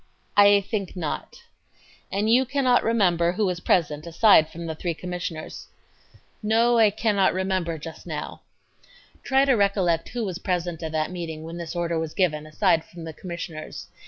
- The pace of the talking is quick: No, average, 185 wpm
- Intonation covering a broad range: No, average, 3.8 semitones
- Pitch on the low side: No, medium, 180 Hz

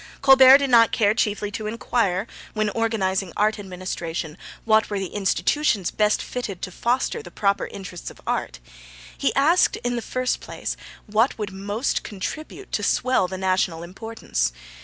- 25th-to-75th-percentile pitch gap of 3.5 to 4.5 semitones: Yes, average, 4.0 semitones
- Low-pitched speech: No, high, 210 Hz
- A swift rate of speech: No, average, 160 wpm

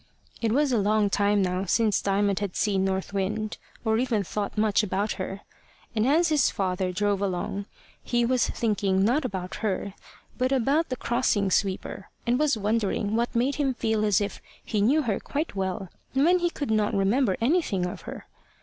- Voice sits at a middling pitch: No, high, 210 Hz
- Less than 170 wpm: No, average, 185 wpm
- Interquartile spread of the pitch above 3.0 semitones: Yes, average, 4.0 semitones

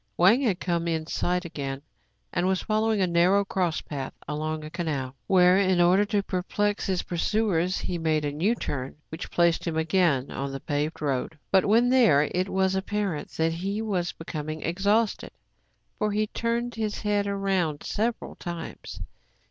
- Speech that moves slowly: No, average, 170 wpm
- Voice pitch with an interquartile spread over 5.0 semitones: No, average, 4.3 semitones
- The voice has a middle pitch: Yes, medium, 180 Hz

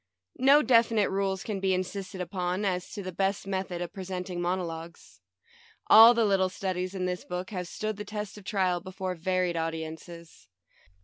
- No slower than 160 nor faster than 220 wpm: Yes, average, 180 wpm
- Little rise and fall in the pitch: Yes, narrow, 1.9 semitones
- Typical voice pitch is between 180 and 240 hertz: Yes, medium, 185 Hz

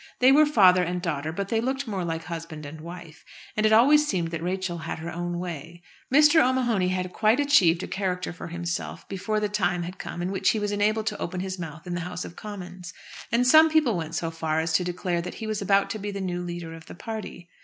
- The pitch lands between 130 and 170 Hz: No, medium, 180 Hz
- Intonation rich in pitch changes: No, average, 3.9 semitones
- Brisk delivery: Yes, fast, 245 wpm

